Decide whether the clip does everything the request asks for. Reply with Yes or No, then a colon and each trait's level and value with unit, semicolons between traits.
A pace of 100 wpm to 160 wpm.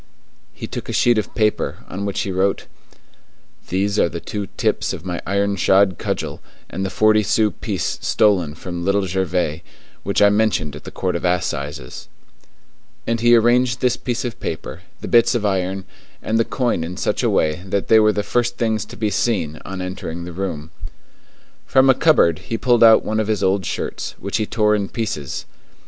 No: average, 195 wpm